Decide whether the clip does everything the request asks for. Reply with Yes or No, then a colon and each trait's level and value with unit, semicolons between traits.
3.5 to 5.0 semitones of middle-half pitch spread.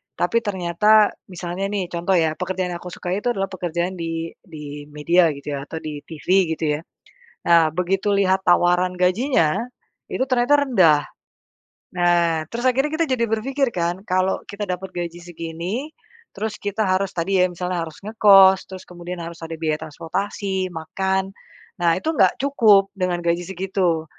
No: average, 2.8 semitones